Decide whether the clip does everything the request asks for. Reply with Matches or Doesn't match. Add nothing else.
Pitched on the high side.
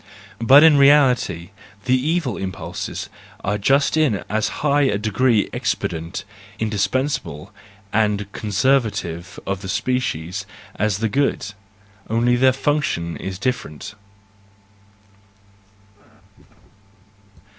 Doesn't match